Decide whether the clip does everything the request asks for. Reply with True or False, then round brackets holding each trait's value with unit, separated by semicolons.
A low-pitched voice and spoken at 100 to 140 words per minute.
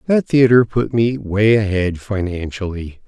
True (105 Hz; 135 wpm)